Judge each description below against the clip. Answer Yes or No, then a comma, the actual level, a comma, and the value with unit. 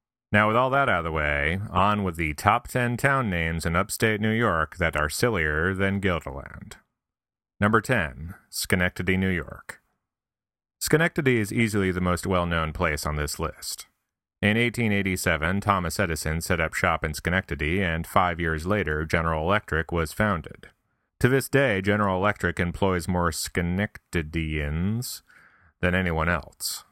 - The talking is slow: No, average, 155 wpm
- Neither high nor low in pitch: No, very low, 90 Hz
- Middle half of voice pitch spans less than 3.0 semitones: No, average, 4.2 semitones